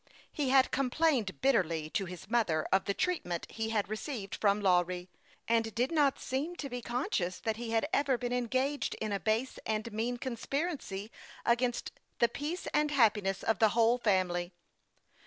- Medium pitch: No, high, 230 Hz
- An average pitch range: Yes, average, 4.9 semitones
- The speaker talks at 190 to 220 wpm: No, average, 175 wpm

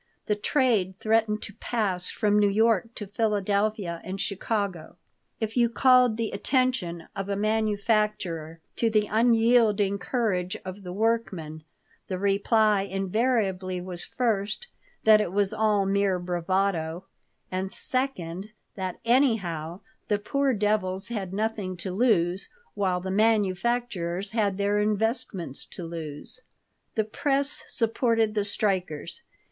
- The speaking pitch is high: Yes, high, 205 Hz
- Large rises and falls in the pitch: No, average, 3.2 semitones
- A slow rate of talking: Yes, slow, 125 wpm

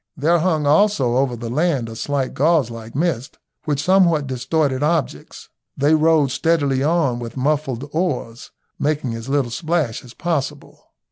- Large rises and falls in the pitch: No, average, 4.2 semitones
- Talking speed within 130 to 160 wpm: Yes, average, 150 wpm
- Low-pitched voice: No, medium, 145 Hz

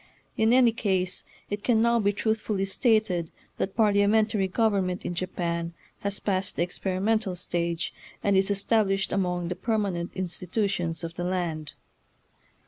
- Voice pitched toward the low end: No, high, 195 Hz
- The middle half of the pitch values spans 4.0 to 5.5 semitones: No, average, 3.2 semitones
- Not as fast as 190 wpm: Yes, average, 140 wpm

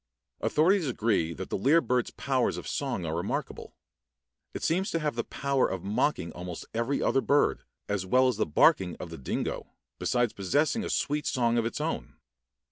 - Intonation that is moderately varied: No, wide, 7.0 semitones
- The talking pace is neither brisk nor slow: Yes, average, 185 wpm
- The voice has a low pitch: Yes, low, 120 Hz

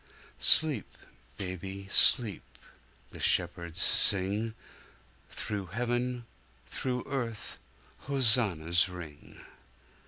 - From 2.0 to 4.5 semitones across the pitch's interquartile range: No, average, 4.9 semitones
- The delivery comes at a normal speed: No, slow, 65 wpm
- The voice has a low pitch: Yes, low, 105 Hz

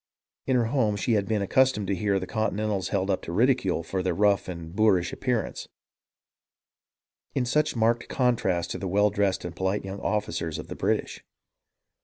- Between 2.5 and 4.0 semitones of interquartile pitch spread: Yes, average, 3.4 semitones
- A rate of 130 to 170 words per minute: No, average, 180 wpm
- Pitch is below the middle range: Yes, low, 100 Hz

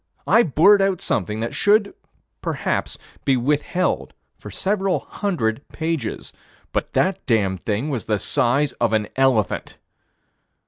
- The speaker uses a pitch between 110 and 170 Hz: Yes, medium, 140 Hz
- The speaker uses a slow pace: Yes, slow, 130 wpm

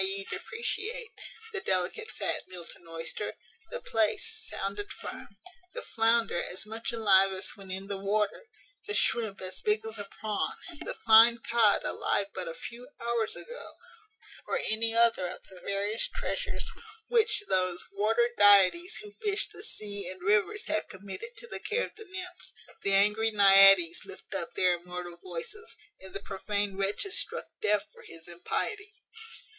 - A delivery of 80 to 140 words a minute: No, average, 165 wpm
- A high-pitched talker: Yes, high, 210 Hz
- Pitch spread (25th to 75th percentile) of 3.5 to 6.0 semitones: Yes, average, 3.9 semitones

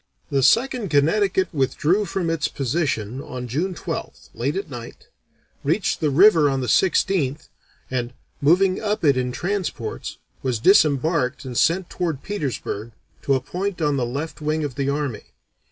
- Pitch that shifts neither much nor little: No, wide, 5.7 semitones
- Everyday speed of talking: Yes, average, 155 wpm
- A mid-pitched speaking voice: Yes, medium, 150 Hz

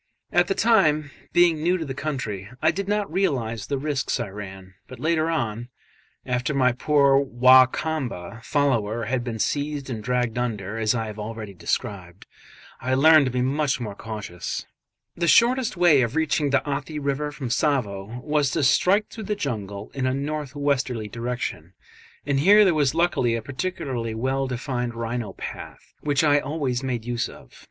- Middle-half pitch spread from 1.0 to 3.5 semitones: No, average, 4.7 semitones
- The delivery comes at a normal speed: Yes, average, 175 wpm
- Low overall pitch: Yes, low, 130 Hz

